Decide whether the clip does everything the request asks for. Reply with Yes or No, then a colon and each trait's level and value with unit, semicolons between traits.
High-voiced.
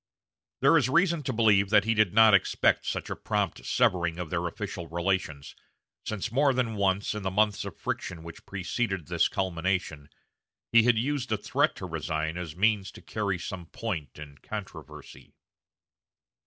No: very low, 95 Hz